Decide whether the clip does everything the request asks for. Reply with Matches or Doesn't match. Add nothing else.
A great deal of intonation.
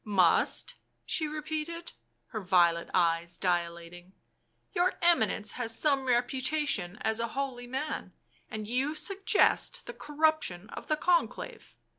Matches